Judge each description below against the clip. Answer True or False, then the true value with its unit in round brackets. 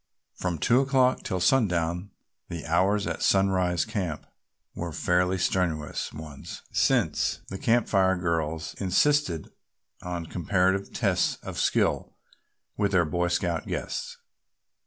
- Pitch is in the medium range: False (90 Hz)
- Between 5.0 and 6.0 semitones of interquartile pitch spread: False (2.6 semitones)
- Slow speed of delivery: True (120 wpm)